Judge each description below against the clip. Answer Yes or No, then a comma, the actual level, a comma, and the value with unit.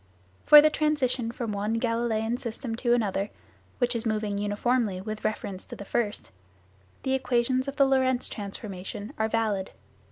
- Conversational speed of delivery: Yes, average, 155 wpm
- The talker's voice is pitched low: No, high, 230 Hz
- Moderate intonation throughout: Yes, average, 3.4 semitones